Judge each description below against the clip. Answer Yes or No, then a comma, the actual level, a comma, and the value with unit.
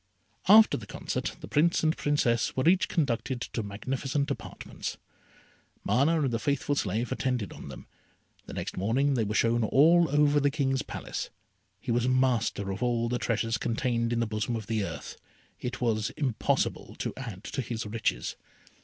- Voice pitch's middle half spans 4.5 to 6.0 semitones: No, average, 3.7 semitones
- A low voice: Yes, low, 125 Hz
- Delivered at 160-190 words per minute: Yes, average, 170 wpm